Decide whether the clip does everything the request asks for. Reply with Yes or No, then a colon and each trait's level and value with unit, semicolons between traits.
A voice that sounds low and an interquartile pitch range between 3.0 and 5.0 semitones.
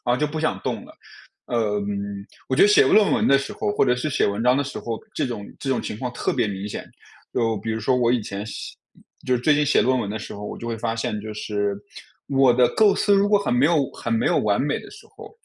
Yes: low, 125 Hz; average, 4.6 semitones